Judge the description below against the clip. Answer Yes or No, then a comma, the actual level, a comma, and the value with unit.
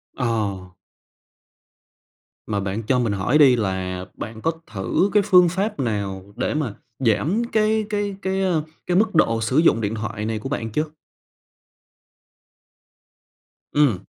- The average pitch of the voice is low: Yes, low, 115 Hz